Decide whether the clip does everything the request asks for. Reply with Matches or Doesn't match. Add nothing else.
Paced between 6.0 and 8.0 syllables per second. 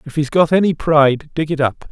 Doesn't match